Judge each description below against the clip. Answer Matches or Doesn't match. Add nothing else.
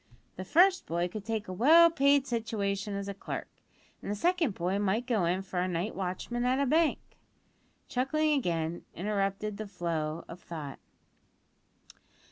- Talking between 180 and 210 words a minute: Doesn't match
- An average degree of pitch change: Doesn't match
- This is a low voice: Doesn't match